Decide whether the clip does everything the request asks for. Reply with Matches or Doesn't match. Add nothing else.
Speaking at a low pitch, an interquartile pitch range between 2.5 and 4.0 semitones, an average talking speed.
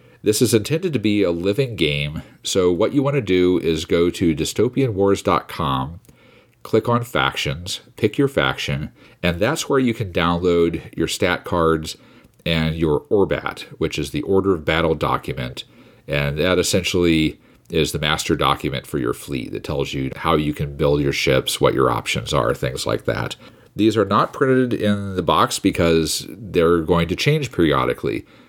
Doesn't match